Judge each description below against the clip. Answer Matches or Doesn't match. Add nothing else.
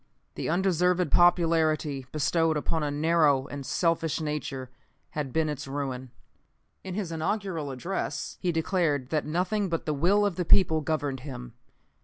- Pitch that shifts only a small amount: Doesn't match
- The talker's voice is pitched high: Doesn't match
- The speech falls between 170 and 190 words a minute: Doesn't match